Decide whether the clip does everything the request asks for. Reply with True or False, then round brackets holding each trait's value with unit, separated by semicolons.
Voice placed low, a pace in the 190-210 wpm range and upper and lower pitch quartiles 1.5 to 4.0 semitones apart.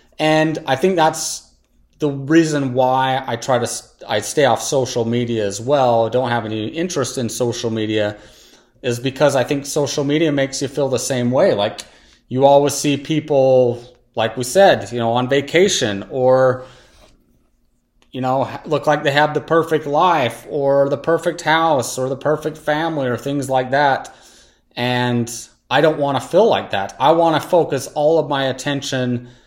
False (130 Hz; 175 wpm; 3.7 semitones)